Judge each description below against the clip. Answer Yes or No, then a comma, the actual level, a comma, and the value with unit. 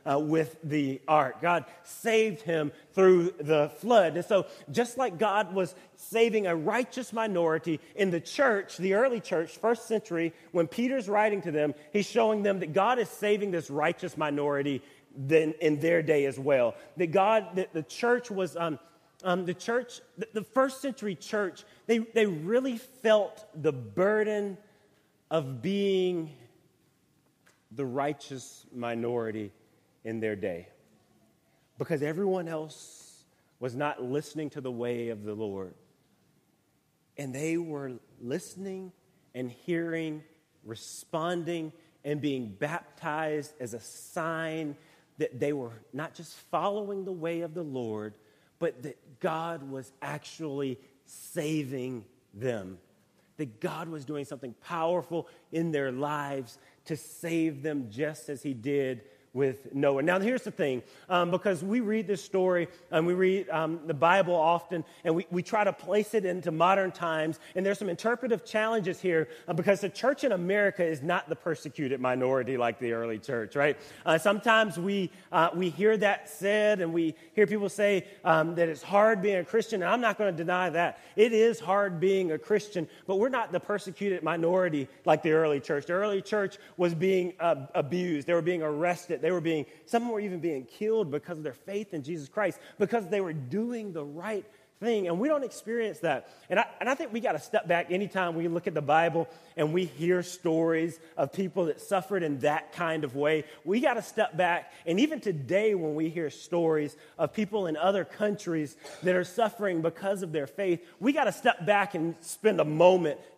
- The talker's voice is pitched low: No, medium, 170 Hz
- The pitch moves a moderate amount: Yes, average, 4.8 semitones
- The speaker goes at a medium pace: Yes, average, 175 wpm